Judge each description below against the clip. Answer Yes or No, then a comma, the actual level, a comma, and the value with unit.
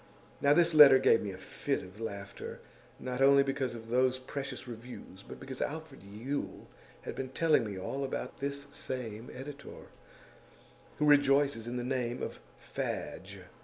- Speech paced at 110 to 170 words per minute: Yes, average, 160 wpm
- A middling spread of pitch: Yes, average, 3.5 semitones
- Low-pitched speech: Yes, low, 130 Hz